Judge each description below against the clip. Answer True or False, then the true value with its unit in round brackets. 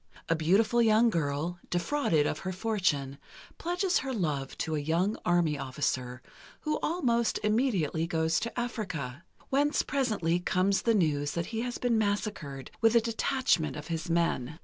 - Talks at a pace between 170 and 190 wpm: False (155 wpm)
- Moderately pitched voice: True (180 Hz)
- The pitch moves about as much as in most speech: False (7.0 semitones)